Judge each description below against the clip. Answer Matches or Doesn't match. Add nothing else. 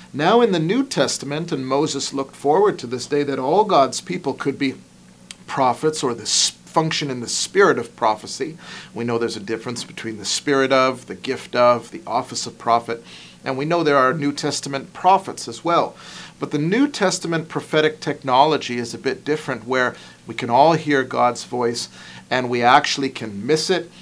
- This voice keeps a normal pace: Matches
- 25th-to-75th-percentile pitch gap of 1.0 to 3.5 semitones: Doesn't match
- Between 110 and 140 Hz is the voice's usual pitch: Matches